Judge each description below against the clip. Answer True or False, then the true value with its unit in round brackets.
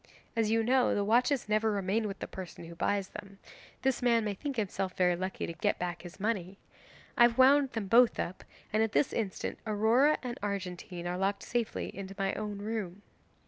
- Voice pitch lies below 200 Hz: False (210 Hz)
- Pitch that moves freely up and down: False (3.4 semitones)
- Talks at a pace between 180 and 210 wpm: True (200 wpm)